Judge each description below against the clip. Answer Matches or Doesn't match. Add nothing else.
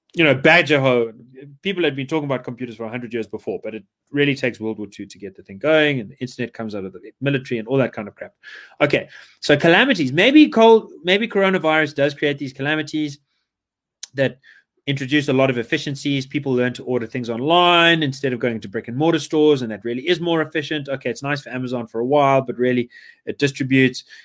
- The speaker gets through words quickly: Matches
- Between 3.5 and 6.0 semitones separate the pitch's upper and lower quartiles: Matches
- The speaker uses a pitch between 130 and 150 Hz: Matches